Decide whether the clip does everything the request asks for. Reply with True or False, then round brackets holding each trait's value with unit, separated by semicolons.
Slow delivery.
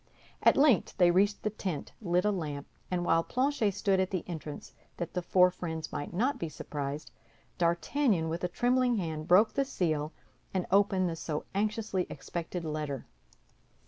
False (170 wpm)